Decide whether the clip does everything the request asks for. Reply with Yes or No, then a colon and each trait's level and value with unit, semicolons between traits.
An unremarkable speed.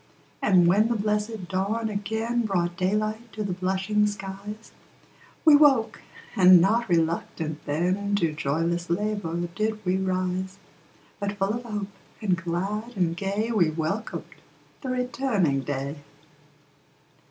No: slow, 130 wpm